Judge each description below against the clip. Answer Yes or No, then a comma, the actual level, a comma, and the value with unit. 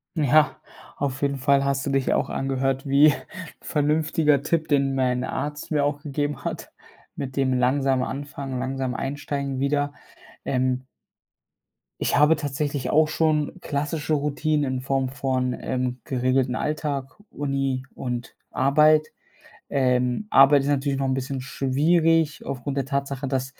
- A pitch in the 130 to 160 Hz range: Yes, medium, 140 Hz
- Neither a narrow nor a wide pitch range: No, narrow, 1.9 semitones